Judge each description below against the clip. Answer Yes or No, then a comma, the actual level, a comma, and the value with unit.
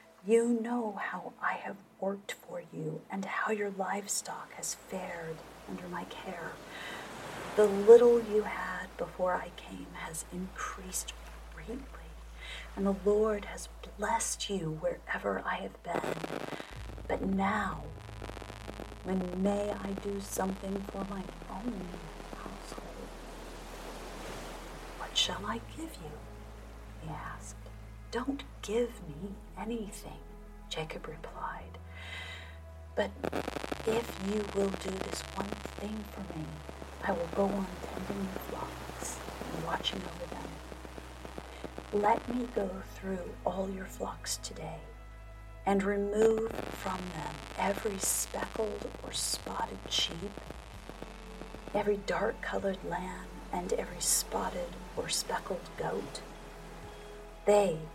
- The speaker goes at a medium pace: No, slow, 115 wpm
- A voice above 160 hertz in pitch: Yes, high, 190 Hz